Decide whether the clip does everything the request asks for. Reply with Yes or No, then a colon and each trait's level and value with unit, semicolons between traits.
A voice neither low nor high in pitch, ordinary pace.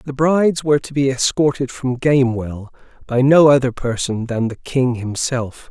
No: low, 130 Hz; average, 170 wpm